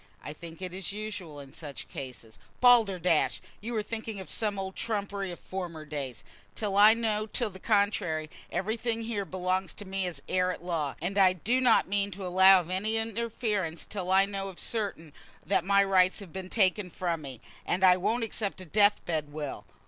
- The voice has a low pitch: No, high, 190 Hz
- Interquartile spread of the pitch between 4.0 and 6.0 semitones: No, average, 3.3 semitones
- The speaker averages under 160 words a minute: No, average, 195 wpm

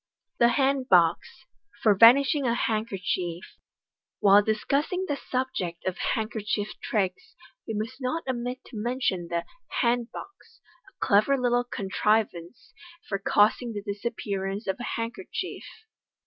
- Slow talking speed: Yes, slow, 130 wpm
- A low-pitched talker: No, high, 225 Hz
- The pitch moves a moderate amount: Yes, average, 4.2 semitones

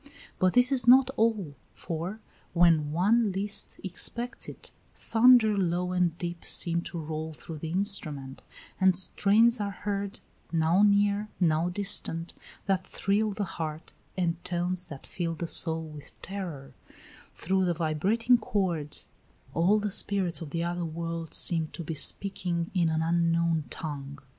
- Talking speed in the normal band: Yes, average, 150 wpm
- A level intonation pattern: No, average, 3.7 semitones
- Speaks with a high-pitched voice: No, medium, 175 Hz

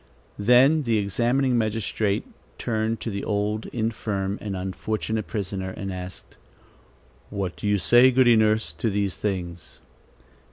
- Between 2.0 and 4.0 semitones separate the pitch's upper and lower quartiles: Yes, average, 2.7 semitones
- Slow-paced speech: Yes, slow, 130 wpm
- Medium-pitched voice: No, low, 105 Hz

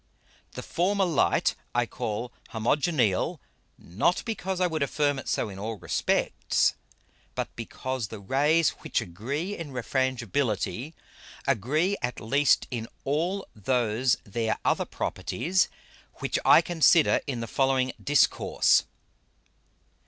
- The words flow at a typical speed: No, slow, 125 wpm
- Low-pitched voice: Yes, low, 130 Hz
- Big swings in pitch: Yes, wide, 5.8 semitones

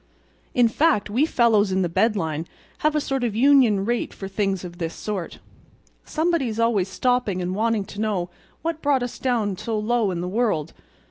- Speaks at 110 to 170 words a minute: No, average, 190 wpm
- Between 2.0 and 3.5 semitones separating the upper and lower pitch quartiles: No, average, 4.4 semitones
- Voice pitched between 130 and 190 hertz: No, high, 215 Hz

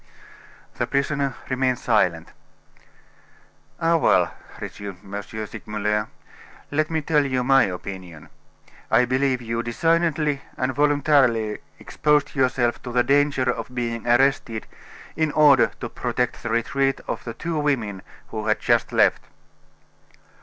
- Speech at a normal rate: No, slow, 125 wpm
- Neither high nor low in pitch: No, low, 130 Hz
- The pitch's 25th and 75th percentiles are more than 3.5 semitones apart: Yes, average, 4.3 semitones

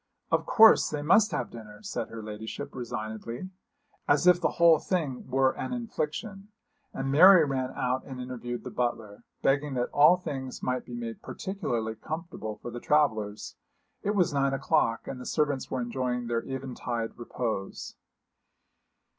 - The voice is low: Yes, low, 130 Hz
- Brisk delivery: No, average, 155 wpm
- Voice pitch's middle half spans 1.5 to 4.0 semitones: No, average, 4.4 semitones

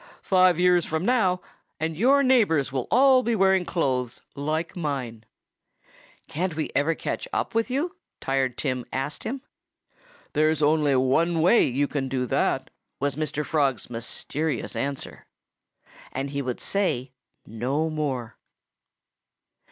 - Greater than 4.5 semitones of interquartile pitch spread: Yes, average, 5.3 semitones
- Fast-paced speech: No, slow, 135 wpm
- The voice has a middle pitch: Yes, medium, 155 Hz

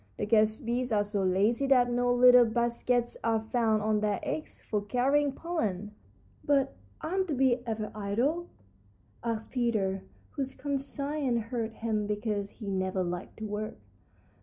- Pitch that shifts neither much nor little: Yes, average, 3.6 semitones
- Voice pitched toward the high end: Yes, high, 230 Hz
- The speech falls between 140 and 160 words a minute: Yes, average, 150 wpm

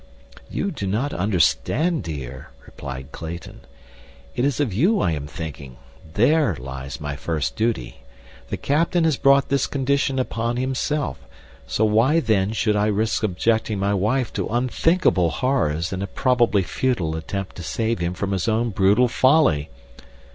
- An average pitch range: No, wide, 7.4 semitones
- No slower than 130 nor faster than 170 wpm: Yes, average, 150 wpm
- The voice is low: Yes, low, 110 Hz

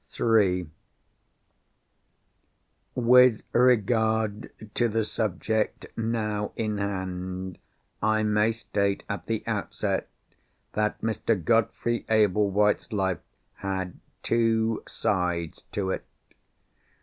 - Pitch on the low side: Yes, low, 105 Hz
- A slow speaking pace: Yes, slow, 90 wpm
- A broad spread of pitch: No, average, 2.7 semitones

